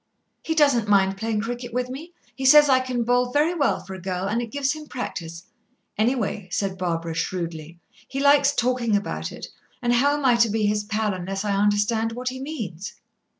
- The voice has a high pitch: Yes, high, 230 Hz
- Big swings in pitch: No, average, 5.0 semitones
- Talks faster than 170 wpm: Yes, average, 200 wpm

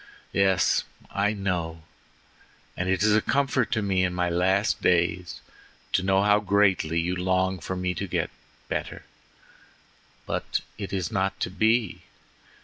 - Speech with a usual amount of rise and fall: No, narrow, 2.1 semitones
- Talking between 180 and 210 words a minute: No, average, 145 wpm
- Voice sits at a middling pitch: No, very low, 95 Hz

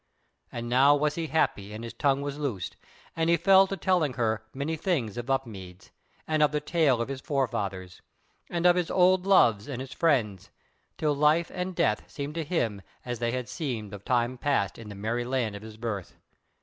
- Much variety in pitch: Yes, wide, 5.9 semitones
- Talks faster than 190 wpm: Yes, average, 200 wpm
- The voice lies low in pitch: Yes, low, 130 Hz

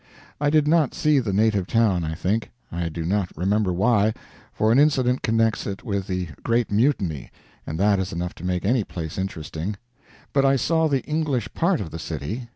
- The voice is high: No, low, 105 Hz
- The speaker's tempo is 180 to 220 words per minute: Yes, average, 195 wpm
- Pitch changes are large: Yes, wide, 6.2 semitones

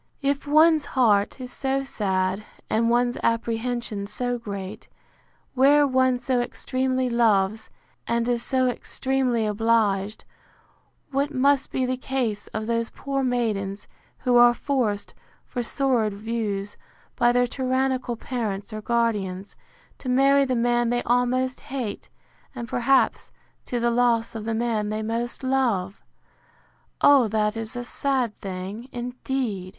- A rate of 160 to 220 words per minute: No, slow, 135 wpm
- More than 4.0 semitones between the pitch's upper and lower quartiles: No, average, 3.1 semitones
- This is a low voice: No, high, 240 Hz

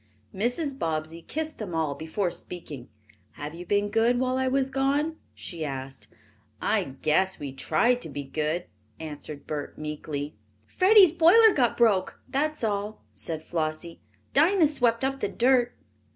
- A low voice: No, high, 205 Hz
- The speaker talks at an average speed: Yes, average, 150 wpm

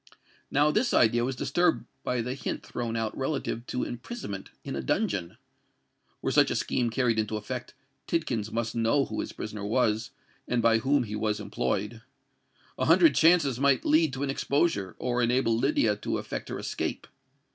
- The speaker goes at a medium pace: Yes, average, 175 wpm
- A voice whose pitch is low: Yes, low, 120 Hz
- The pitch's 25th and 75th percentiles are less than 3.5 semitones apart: No, average, 3.8 semitones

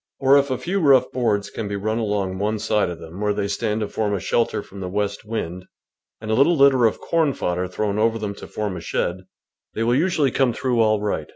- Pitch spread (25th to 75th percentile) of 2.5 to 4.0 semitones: Yes, average, 3.6 semitones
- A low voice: Yes, low, 110 Hz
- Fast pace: Yes, fast, 250 wpm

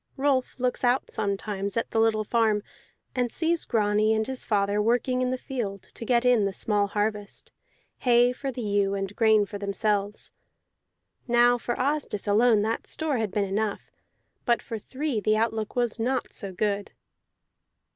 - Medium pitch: No, high, 220 Hz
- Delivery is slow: No, average, 165 wpm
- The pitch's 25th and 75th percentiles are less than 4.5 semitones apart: Yes, average, 3.1 semitones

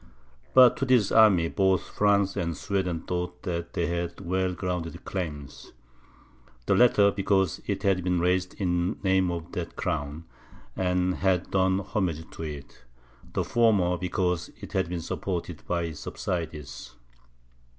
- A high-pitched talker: No, very low, 90 Hz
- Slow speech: No, average, 145 wpm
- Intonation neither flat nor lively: No, narrow, 2.2 semitones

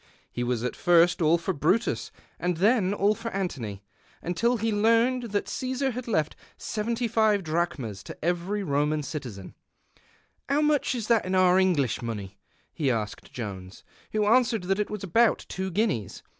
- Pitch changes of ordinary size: No, wide, 7.3 semitones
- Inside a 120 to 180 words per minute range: Yes, average, 170 wpm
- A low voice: No, medium, 185 Hz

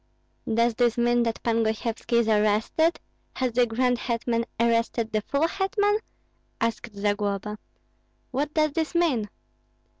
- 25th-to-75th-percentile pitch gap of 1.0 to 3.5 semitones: Yes, average, 2.9 semitones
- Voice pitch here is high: Yes, high, 235 Hz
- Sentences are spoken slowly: Yes, slow, 130 wpm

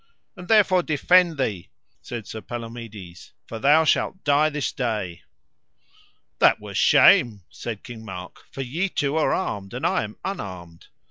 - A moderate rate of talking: Yes, average, 150 wpm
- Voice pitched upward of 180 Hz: No, low, 120 Hz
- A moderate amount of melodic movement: No, wide, 7.0 semitones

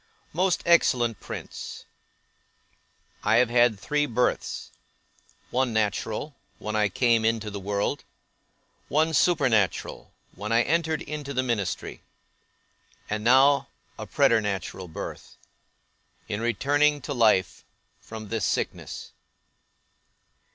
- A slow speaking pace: Yes, slow, 105 wpm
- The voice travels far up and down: No, average, 4.9 semitones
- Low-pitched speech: Yes, low, 120 Hz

